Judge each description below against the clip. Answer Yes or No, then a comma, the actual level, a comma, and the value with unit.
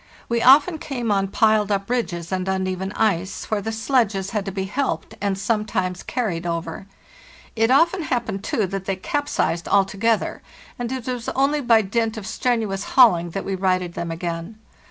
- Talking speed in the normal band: Yes, average, 175 wpm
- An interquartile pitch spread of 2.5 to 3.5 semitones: No, average, 3.9 semitones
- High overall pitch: Yes, high, 205 Hz